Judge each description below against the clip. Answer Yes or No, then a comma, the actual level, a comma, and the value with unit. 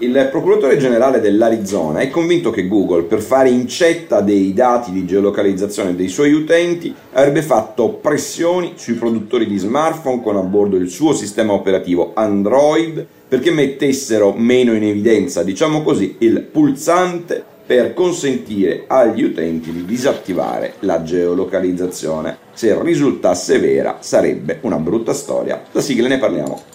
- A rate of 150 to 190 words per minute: No, average, 135 wpm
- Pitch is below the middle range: Yes, low, 115 Hz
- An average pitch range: No, wide, 8.8 semitones